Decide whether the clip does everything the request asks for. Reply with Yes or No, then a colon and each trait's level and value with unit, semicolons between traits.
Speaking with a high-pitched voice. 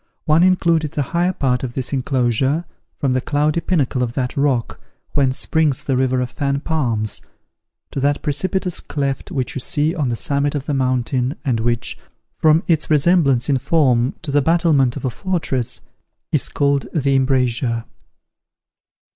No: medium, 140 Hz